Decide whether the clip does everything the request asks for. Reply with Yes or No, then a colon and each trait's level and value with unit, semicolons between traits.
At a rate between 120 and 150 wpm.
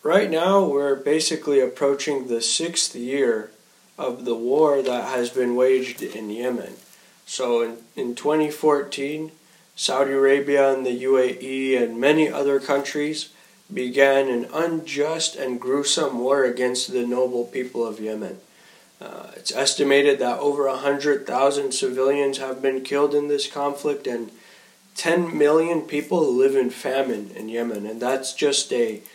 Yes: average, 145 wpm